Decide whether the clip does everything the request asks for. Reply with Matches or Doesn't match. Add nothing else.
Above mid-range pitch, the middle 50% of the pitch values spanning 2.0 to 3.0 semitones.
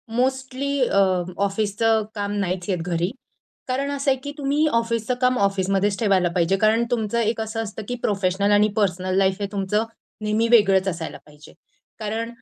Doesn't match